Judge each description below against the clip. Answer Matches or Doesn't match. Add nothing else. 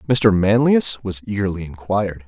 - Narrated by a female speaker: Doesn't match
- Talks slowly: Matches